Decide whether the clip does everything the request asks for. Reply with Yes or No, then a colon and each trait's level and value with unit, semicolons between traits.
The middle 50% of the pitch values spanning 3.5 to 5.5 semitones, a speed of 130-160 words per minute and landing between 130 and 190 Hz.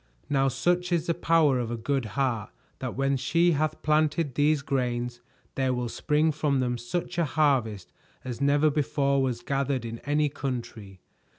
No: average, 3.8 semitones; average, 170 wpm; low, 135 Hz